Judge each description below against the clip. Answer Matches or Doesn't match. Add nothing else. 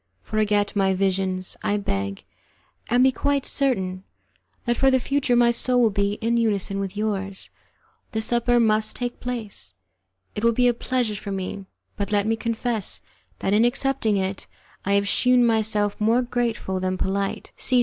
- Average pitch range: Matches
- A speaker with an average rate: Matches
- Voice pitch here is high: Matches